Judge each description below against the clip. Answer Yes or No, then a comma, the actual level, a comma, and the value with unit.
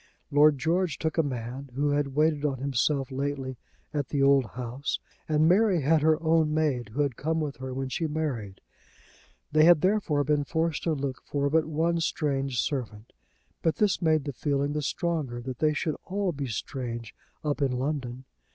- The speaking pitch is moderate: Yes, medium, 145 Hz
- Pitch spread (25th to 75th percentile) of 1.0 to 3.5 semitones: Yes, average, 3.0 semitones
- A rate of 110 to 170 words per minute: No, average, 185 wpm